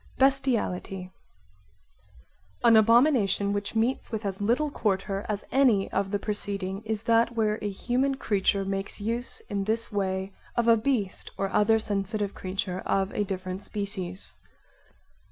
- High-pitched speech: Yes, high, 205 Hz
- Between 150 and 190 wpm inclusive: No, average, 140 wpm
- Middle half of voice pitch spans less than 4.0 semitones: Yes, average, 2.9 semitones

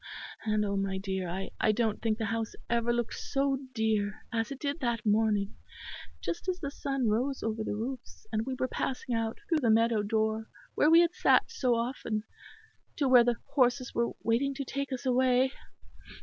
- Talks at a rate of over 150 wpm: Yes, average, 190 wpm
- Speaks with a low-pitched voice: No, high, 235 Hz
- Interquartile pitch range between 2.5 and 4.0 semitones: Yes, average, 3.4 semitones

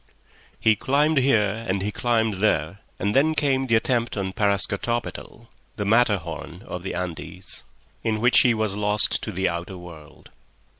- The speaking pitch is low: Yes, low, 105 Hz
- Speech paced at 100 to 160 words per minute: Yes, average, 155 wpm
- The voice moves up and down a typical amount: Yes, average, 3.9 semitones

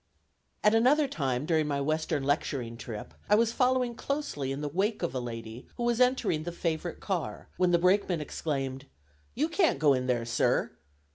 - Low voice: No, medium, 160 Hz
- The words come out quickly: No, average, 185 wpm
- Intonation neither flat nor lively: No, wide, 8.8 semitones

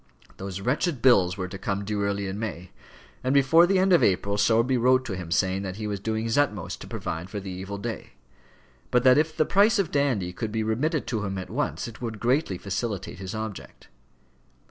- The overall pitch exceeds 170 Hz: No, low, 110 Hz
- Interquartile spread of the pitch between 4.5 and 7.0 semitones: Yes, average, 5.0 semitones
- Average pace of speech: No, fast, 215 wpm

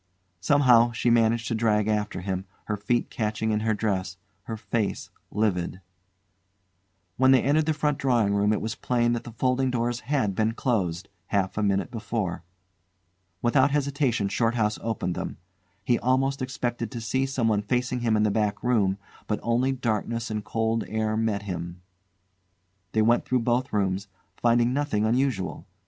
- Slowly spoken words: No, average, 160 wpm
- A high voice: No, low, 115 Hz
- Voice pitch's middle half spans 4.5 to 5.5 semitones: No, average, 2.8 semitones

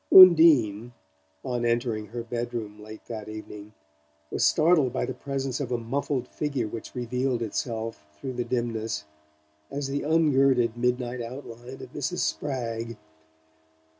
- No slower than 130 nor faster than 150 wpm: Yes, slow, 135 wpm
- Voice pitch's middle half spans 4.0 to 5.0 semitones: No, average, 2.9 semitones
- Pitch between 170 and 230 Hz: No, low, 120 Hz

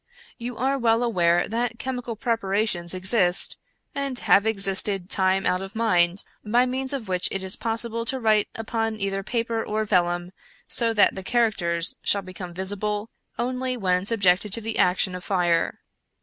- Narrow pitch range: No, average, 3.9 semitones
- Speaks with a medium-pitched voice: No, high, 210 Hz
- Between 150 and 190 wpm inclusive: Yes, average, 165 wpm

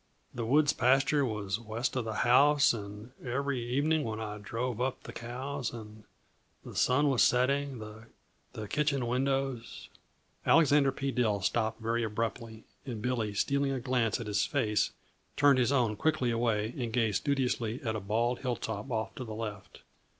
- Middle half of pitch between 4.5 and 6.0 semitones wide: No, average, 3.5 semitones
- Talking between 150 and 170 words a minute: Yes, average, 165 wpm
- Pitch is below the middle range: Yes, low, 120 Hz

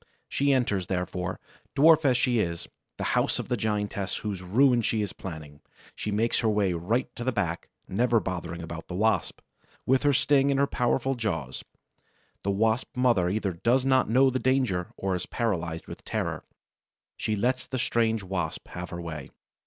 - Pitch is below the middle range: Yes, low, 110 Hz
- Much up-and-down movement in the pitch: Yes, wide, 5.8 semitones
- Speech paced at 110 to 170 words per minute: No, average, 180 wpm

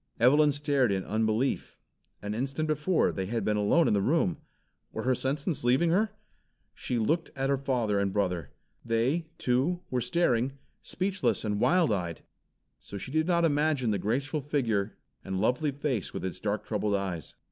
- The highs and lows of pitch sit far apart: Yes, wide, 6.2 semitones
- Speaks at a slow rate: No, average, 170 wpm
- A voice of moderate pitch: No, low, 125 Hz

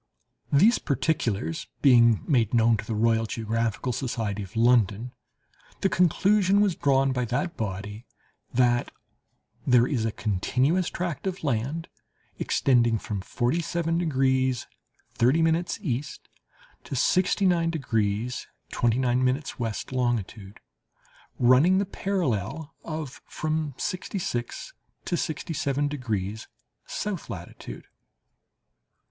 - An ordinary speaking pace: No, slow, 105 wpm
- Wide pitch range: Yes, wide, 6.1 semitones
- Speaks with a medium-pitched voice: No, low, 125 Hz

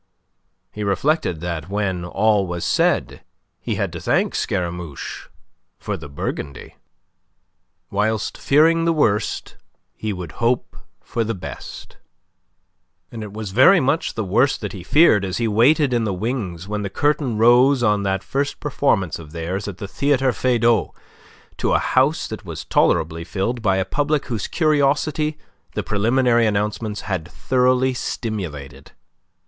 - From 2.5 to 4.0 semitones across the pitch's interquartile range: No, wide, 5.5 semitones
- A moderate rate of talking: Yes, average, 150 wpm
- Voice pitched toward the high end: No, low, 110 Hz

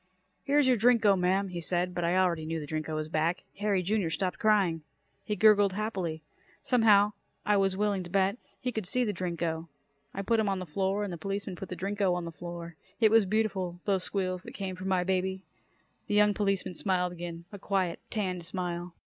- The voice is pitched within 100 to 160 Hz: No, high, 190 Hz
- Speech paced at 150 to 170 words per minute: No, fast, 205 wpm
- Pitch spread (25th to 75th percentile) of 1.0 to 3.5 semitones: Yes, average, 2.8 semitones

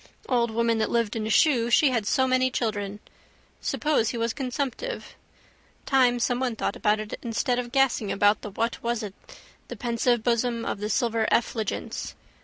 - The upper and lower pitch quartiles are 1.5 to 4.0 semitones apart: Yes, narrow, 2.4 semitones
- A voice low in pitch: No, high, 235 Hz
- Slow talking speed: No, average, 175 wpm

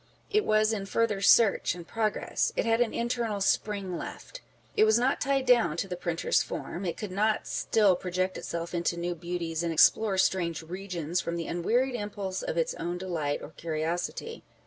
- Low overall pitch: No, medium, 185 Hz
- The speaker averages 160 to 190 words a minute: Yes, average, 180 wpm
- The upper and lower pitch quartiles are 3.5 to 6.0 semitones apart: Yes, average, 4.1 semitones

